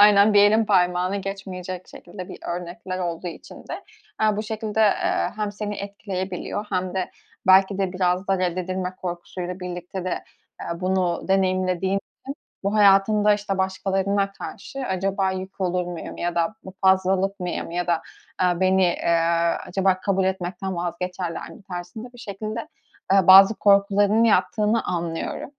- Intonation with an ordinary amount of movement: No, narrow, 1.9 semitones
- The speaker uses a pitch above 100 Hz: Yes, high, 190 Hz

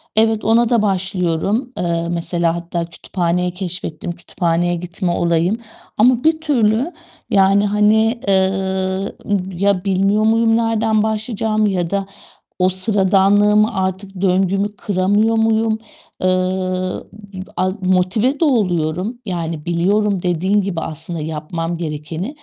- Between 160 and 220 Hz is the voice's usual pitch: Yes, high, 190 Hz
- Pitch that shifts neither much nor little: Yes, average, 3.6 semitones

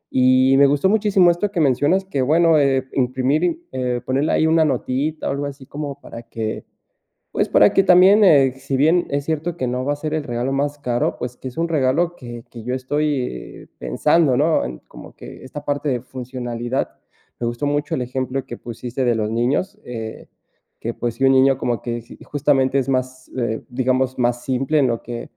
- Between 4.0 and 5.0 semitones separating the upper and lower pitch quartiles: No, average, 3.3 semitones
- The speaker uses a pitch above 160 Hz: No, low, 135 Hz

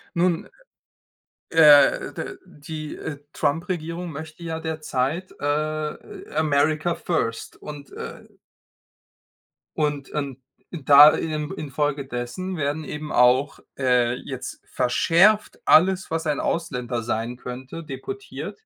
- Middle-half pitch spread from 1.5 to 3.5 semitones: Yes, average, 2.9 semitones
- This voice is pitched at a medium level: Yes, medium, 150 Hz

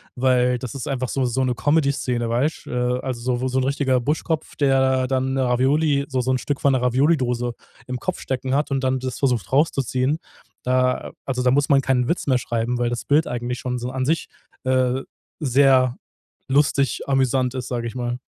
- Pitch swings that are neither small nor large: No, narrow, 1.7 semitones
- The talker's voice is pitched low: Yes, low, 130 Hz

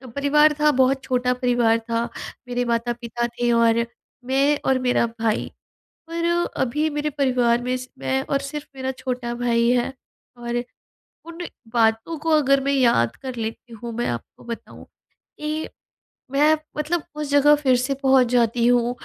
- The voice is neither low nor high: No, very high, 250 Hz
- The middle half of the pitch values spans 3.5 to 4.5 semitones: No, average, 3.1 semitones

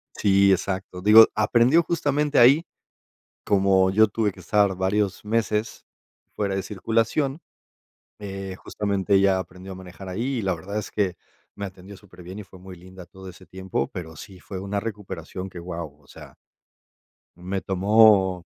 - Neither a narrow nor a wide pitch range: No, narrow, 2.3 semitones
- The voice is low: Yes, very low, 95 Hz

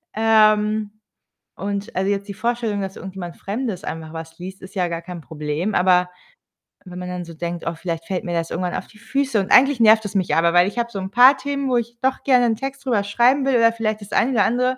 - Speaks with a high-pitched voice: Yes, high, 205 Hz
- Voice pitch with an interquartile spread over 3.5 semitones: Yes, average, 4.7 semitones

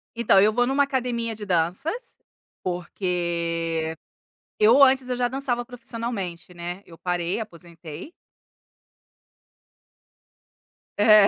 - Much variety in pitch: Yes, wide, 6.1 semitones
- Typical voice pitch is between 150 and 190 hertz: No, high, 205 Hz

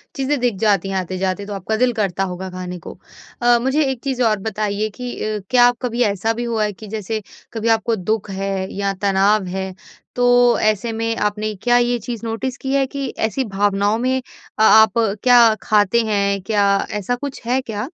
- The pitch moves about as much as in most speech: Yes, average, 3.3 semitones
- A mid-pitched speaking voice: No, high, 220 Hz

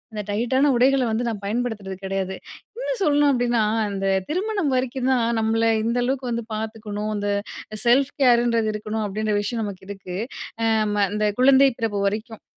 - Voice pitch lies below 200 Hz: No, high, 230 Hz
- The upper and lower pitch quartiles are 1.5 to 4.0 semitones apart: Yes, average, 3.4 semitones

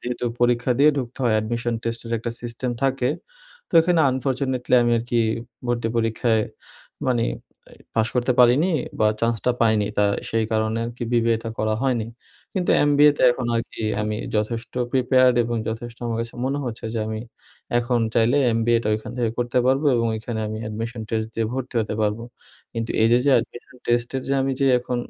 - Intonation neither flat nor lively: No, narrow, 1.9 semitones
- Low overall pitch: Yes, low, 120 Hz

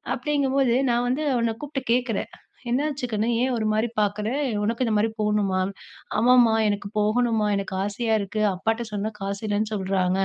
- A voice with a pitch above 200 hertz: Yes, high, 220 Hz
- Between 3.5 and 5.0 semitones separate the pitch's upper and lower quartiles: No, average, 3.0 semitones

